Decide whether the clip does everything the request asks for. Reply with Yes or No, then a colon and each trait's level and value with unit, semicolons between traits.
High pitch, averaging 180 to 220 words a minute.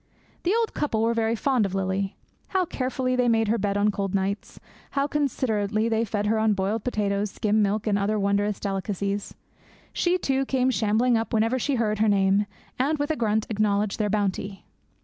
Yes: high, 215 Hz; average, 190 wpm